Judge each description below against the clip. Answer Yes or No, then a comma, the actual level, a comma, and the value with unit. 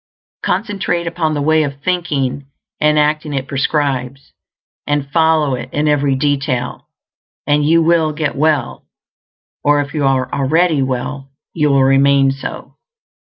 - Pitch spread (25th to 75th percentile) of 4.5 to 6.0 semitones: No, narrow, 2.4 semitones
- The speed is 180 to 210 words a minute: No, average, 140 wpm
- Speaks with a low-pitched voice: No, medium, 145 Hz